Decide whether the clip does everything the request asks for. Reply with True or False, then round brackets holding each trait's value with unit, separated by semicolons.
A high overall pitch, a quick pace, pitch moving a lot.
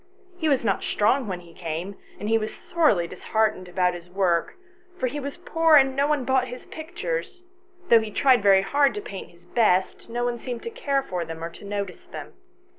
True (225 Hz; 210 wpm; 7.3 semitones)